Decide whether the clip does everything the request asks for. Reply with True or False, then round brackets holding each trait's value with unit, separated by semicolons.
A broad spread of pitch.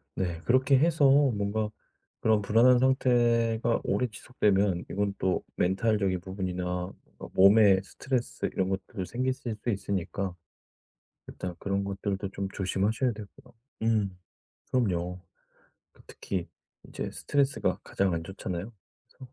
False (3.9 semitones)